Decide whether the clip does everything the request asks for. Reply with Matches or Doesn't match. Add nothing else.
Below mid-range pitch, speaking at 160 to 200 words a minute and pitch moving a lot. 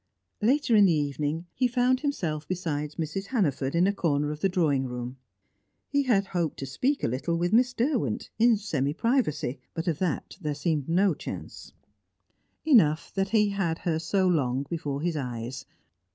Doesn't match